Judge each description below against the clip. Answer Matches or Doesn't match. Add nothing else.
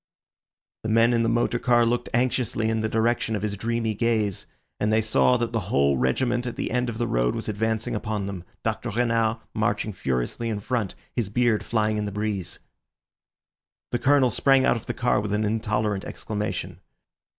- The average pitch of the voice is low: Matches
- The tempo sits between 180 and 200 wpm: Matches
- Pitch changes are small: Matches